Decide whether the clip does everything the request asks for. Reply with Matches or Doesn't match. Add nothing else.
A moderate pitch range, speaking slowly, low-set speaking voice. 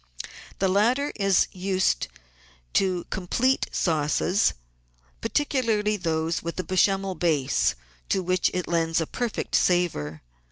Doesn't match